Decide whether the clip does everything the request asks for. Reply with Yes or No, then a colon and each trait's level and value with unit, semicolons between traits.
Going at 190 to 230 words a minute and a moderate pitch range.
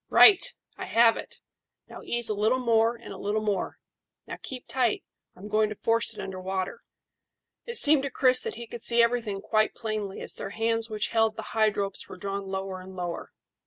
Yes: fast, 205 wpm; average, 3.0 semitones